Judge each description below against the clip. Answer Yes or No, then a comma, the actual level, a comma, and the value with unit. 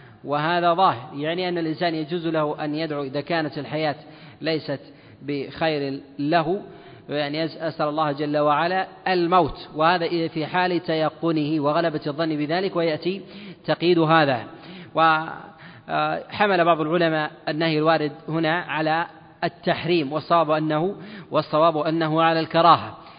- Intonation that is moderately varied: No, narrow, 2.0 semitones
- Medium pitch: Yes, medium, 160 Hz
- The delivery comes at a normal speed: Yes, average, 115 wpm